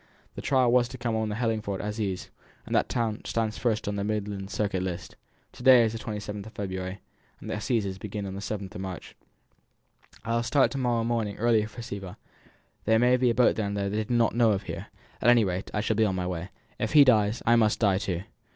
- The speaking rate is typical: No, fast, 235 wpm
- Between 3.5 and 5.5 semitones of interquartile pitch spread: No, average, 2.9 semitones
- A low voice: Yes, low, 105 Hz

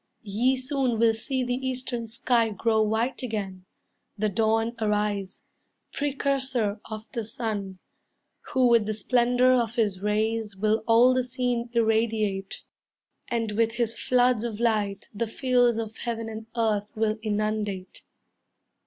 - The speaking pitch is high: Yes, high, 225 Hz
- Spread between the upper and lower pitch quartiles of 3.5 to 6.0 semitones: No, narrow, 2.4 semitones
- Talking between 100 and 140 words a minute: Yes, slow, 135 wpm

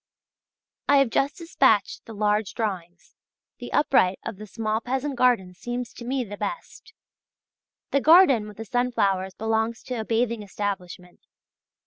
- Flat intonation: No, average, 3.7 semitones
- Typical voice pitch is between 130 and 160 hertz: No, high, 225 Hz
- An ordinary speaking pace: Yes, average, 145 wpm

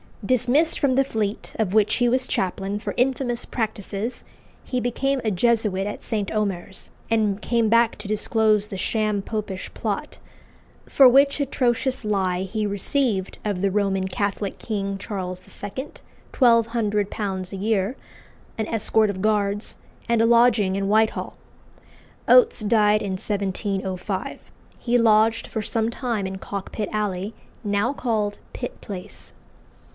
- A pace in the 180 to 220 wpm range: No, average, 140 wpm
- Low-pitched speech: No, high, 215 Hz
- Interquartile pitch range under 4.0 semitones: Yes, average, 2.9 semitones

